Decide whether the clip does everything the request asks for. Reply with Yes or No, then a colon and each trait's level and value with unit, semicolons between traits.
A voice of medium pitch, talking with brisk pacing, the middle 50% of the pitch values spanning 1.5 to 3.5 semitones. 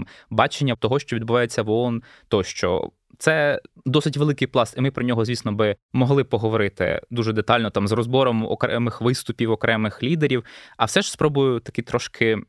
No: low, 120 Hz; fast, 165 wpm; average, 2.9 semitones